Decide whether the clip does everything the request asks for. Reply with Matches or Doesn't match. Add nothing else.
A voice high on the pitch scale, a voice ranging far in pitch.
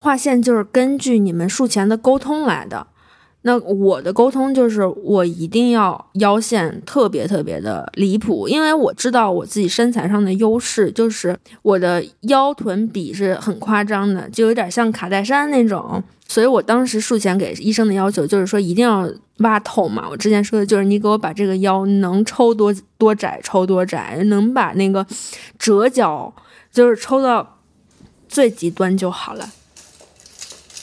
Doesn't match